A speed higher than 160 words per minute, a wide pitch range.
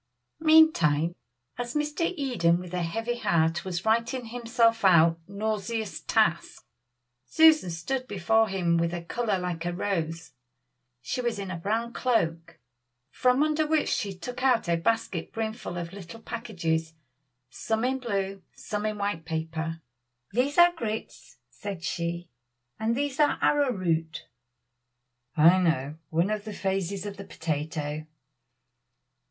No: slow, 135 wpm; wide, 5.8 semitones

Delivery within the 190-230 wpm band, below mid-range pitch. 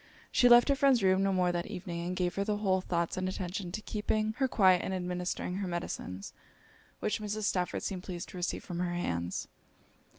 No: average, 200 wpm; medium, 185 Hz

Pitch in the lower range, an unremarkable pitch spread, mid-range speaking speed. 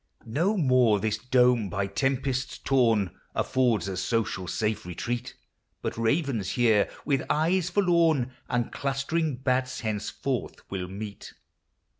No: low, 125 Hz; average, 4.3 semitones; slow, 120 wpm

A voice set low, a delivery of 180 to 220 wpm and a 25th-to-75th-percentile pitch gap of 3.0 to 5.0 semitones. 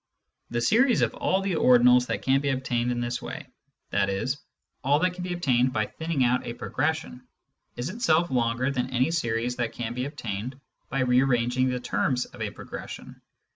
Yes: low, 125 Hz; average, 185 wpm; average, 3.3 semitones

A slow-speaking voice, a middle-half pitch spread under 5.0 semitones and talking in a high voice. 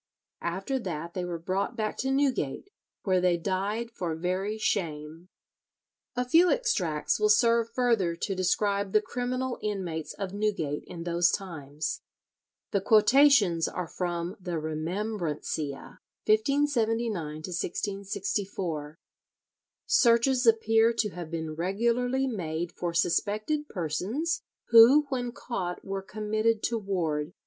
No: slow, 120 wpm; average, 5.3 semitones; high, 195 Hz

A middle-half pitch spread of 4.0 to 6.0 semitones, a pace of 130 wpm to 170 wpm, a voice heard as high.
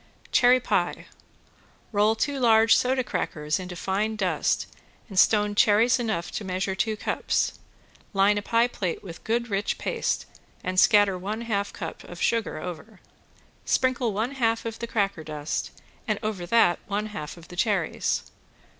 No: average, 3.6 semitones; average, 155 wpm; high, 210 Hz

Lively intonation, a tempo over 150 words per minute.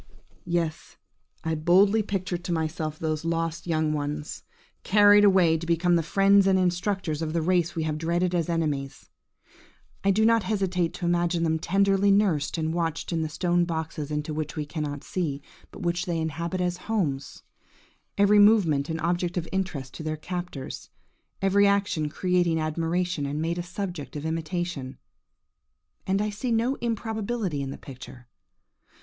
No: average, 3.3 semitones; average, 160 wpm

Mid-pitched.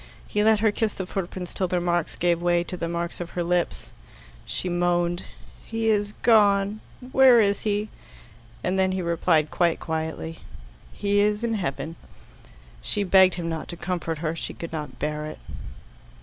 Yes: medium, 175 Hz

